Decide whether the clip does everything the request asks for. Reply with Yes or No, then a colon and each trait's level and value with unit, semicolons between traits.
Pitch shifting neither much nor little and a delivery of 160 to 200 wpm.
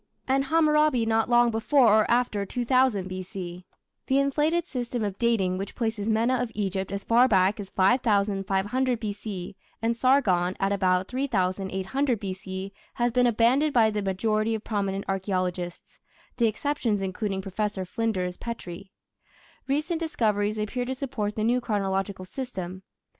No: average, 4.3 semitones; average, 140 wpm